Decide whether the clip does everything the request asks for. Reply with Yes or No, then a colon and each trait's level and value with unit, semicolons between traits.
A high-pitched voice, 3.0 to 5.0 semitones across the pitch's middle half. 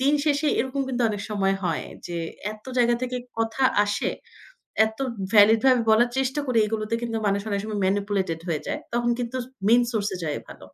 Yes: high, 225 Hz; average, 3.5 semitones